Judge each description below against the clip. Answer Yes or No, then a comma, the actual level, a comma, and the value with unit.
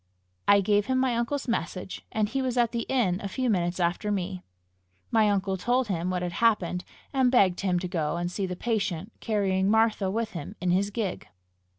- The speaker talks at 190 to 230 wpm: Yes, fast, 205 wpm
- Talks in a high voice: Yes, high, 200 Hz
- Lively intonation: No, average, 4.2 semitones